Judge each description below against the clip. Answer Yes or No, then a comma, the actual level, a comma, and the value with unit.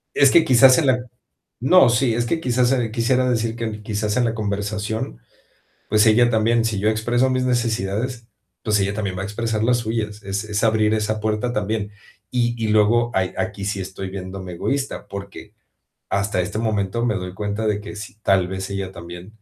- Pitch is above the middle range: No, low, 110 Hz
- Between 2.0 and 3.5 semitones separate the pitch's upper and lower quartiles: Yes, average, 2.8 semitones